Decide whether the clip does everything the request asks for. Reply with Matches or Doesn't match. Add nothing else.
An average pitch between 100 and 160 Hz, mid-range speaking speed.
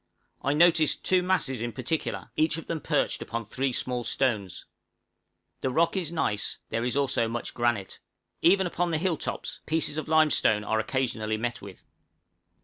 Matches